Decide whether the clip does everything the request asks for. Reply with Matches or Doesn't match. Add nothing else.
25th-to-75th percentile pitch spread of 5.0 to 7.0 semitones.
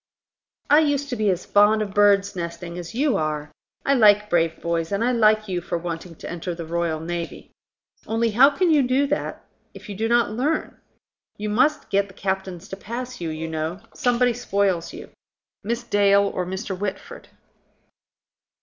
Matches